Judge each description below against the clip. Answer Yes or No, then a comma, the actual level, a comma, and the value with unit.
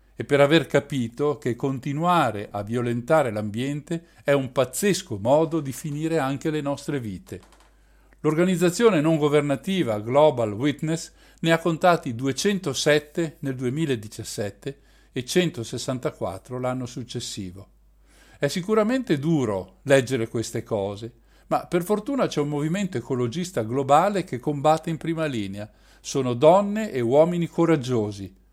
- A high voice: No, medium, 140 Hz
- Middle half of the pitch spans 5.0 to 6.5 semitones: Yes, average, 5.3 semitones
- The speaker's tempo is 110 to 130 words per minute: Yes, average, 120 wpm